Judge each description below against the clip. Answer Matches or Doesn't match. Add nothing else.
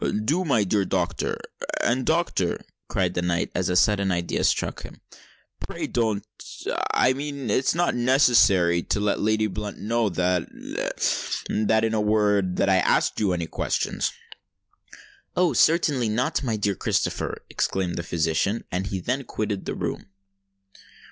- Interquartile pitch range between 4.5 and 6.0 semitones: Matches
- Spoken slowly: Doesn't match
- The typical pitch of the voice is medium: Doesn't match